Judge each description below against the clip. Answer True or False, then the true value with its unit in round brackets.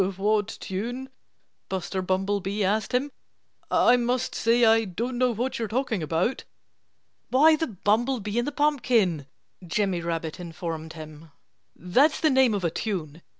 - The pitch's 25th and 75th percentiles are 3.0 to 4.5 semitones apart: False (5.6 semitones)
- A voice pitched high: True (210 Hz)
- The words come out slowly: False (145 wpm)